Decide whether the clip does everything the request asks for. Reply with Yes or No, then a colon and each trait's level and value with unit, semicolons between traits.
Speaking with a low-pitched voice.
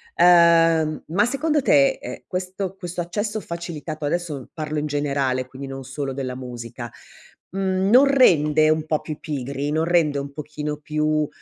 No: medium, 155 Hz